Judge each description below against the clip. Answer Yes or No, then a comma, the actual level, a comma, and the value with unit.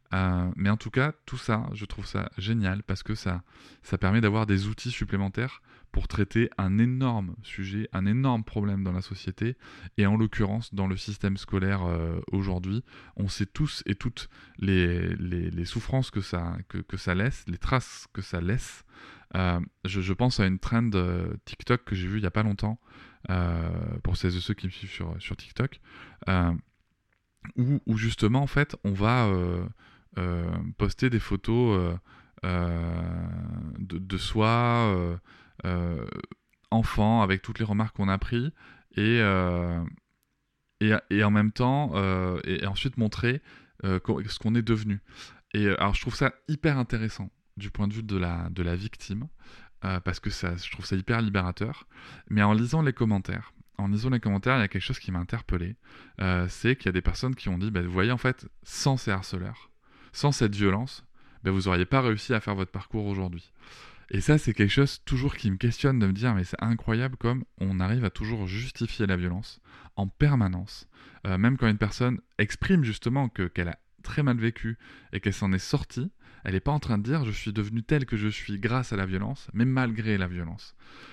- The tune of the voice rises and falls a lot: No, average, 3.8 semitones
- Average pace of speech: Yes, average, 200 wpm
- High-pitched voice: No, low, 105 Hz